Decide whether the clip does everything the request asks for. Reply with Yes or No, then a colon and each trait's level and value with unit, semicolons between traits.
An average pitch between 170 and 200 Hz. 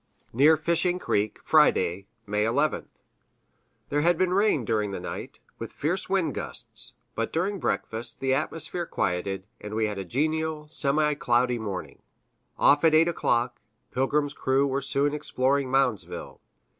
No: low, 135 Hz